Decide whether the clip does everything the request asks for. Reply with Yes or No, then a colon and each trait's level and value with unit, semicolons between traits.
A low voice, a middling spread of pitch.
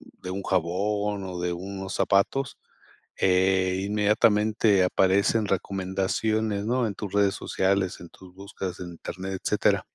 No: very low, 95 Hz; narrow, 1.9 semitones